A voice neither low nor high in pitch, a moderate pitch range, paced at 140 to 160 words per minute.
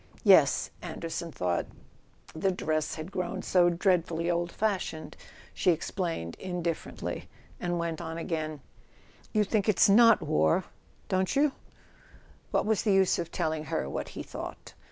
Yes: medium, 175 Hz; average, 3.2 semitones; average, 145 wpm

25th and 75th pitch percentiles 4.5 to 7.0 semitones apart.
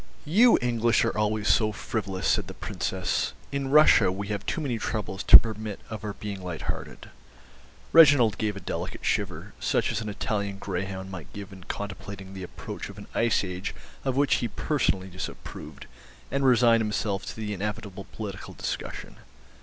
No: average, 3.2 semitones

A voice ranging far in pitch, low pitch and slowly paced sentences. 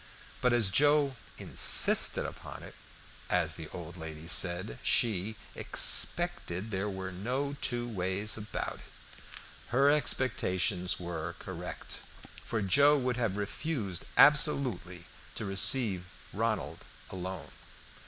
Yes: wide, 5.9 semitones; low, 100 Hz; slow, 115 wpm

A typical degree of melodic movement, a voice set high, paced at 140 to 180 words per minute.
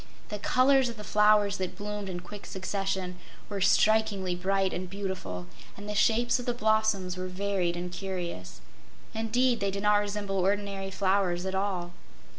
No: narrow, 2.2 semitones; high, 195 Hz; average, 165 wpm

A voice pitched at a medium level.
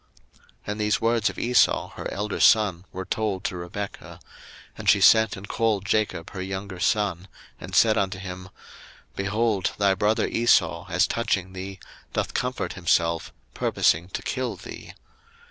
No: low, 100 Hz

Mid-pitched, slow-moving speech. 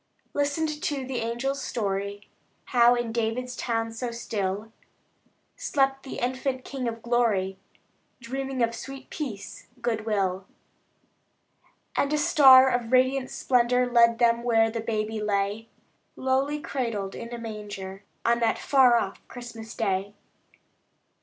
No: high, 235 Hz; slow, 130 wpm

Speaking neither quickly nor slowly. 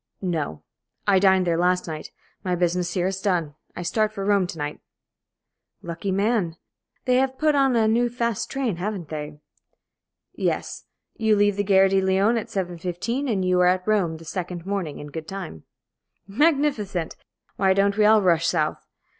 Yes: average, 175 wpm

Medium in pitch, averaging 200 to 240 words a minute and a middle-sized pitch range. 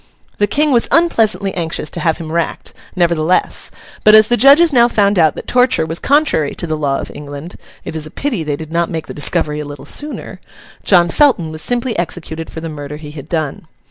No: medium, 170 Hz; fast, 205 wpm; wide, 6.5 semitones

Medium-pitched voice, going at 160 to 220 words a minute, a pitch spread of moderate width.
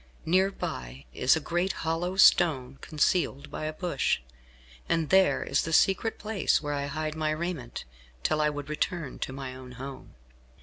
Yes: medium, 155 Hz; average, 170 wpm; average, 4.2 semitones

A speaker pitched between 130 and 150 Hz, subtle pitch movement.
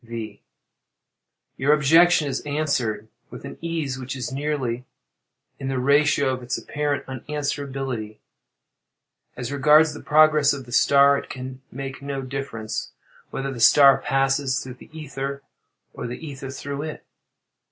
Yes: low, 135 Hz; narrow, 2.2 semitones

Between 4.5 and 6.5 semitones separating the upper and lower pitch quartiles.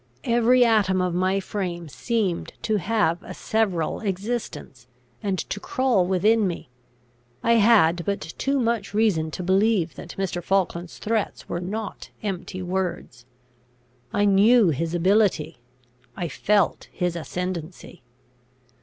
No: average, 3.9 semitones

